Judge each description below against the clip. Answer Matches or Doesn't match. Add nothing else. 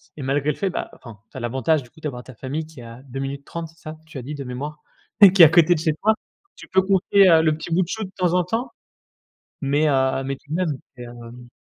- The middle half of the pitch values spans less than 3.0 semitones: Doesn't match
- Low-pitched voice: Doesn't match